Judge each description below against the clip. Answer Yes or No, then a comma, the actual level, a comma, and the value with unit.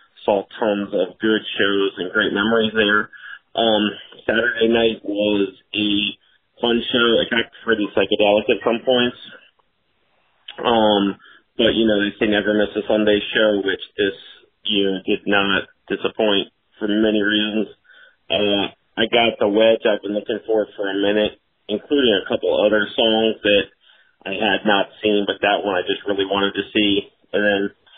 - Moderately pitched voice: No, low, 105 Hz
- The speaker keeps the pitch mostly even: Yes, narrow, 1.6 semitones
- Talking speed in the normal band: Yes, average, 165 wpm